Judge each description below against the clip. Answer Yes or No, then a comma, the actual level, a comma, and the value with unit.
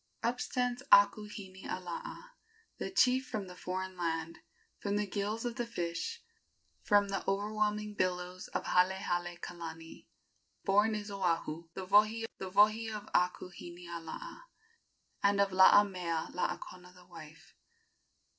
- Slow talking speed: Yes, slow, 115 wpm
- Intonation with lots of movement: No, average, 3.1 semitones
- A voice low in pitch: No, high, 195 Hz